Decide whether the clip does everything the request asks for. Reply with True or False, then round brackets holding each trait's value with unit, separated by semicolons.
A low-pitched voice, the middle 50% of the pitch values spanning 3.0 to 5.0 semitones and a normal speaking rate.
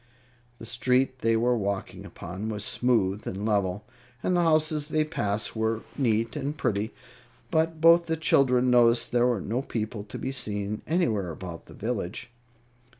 True (115 Hz; 4.6 semitones; 160 wpm)